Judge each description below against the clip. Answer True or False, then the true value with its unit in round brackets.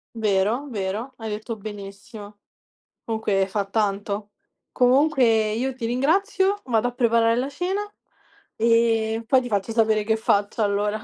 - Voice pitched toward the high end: True (225 Hz)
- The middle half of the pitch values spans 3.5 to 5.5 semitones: False (3.1 semitones)